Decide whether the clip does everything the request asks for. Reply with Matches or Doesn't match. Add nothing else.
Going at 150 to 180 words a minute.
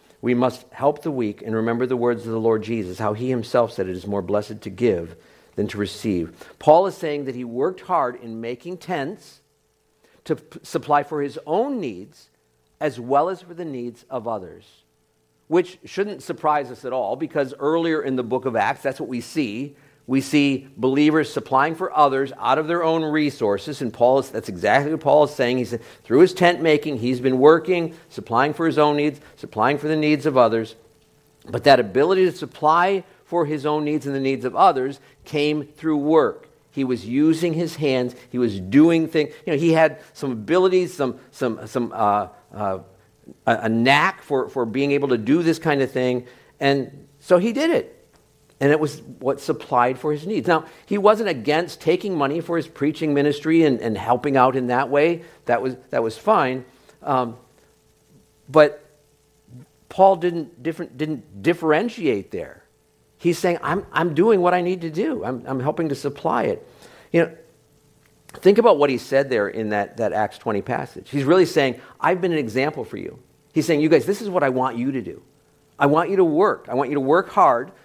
Doesn't match